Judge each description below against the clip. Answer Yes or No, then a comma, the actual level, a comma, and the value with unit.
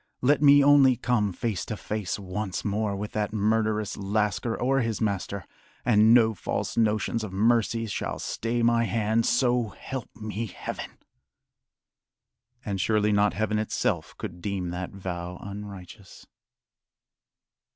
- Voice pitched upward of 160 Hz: No, low, 105 Hz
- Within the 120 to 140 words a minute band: Yes, slow, 135 wpm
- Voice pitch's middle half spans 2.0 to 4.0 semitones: Yes, narrow, 2.5 semitones